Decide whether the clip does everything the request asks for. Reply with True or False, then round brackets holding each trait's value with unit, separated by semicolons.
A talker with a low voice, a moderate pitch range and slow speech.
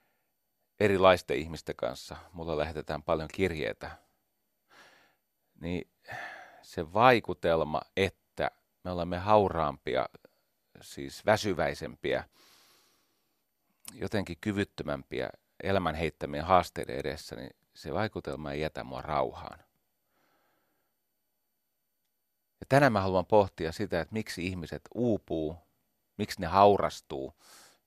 True (90 Hz; 4.1 semitones; 90 wpm)